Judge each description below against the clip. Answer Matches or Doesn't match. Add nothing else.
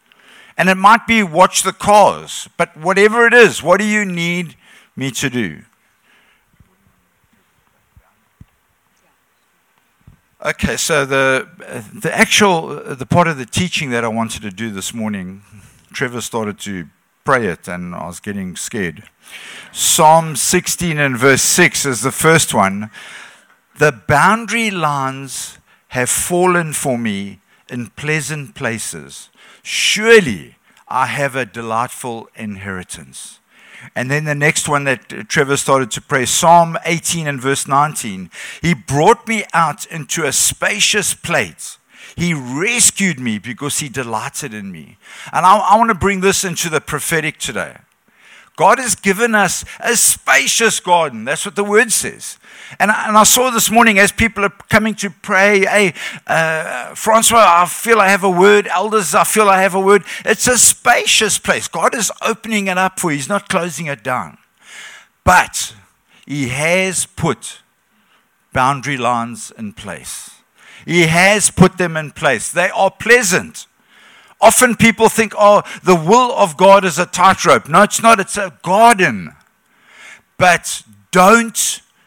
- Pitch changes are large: Matches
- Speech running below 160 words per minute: Matches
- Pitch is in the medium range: Matches